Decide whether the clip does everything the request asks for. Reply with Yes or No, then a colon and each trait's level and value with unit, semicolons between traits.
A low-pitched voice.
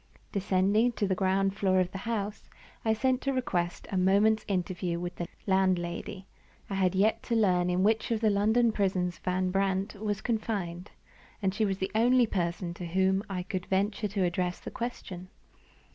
No: high, 195 Hz